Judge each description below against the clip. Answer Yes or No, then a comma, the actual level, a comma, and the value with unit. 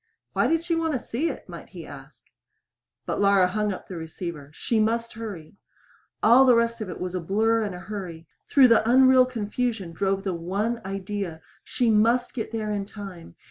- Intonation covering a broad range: No, average, 3.8 semitones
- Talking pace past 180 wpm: Yes, average, 195 wpm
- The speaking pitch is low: No, high, 210 Hz